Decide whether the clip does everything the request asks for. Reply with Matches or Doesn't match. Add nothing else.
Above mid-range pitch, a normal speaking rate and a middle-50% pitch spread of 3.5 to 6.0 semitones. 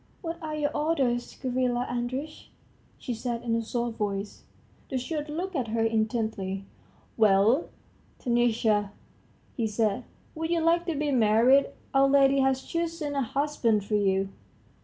Matches